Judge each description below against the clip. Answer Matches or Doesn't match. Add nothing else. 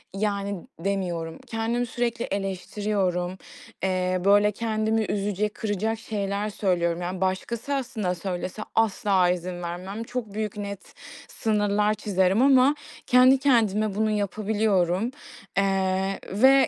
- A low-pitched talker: Doesn't match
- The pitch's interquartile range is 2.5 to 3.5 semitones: Matches